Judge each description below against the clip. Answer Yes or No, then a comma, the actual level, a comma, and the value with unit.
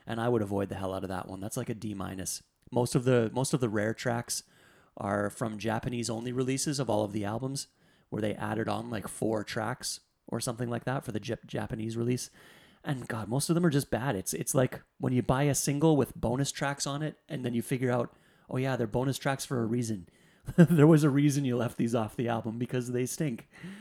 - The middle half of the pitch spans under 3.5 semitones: No, average, 3.8 semitones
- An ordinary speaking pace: No, fast, 240 wpm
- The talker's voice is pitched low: Yes, low, 125 Hz